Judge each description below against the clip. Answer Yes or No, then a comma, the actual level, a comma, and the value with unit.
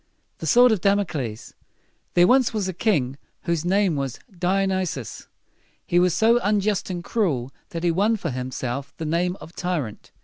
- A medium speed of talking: Yes, average, 180 wpm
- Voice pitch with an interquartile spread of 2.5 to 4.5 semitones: No, wide, 5.6 semitones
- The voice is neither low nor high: Yes, medium, 175 Hz